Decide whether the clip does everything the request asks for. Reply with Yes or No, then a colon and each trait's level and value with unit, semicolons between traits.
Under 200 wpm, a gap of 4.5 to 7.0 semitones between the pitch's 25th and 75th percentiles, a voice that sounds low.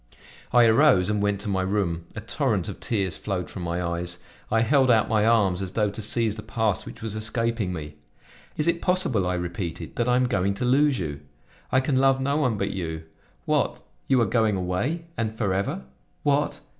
No: fast, 205 wpm; average, 5.1 semitones; low, 105 Hz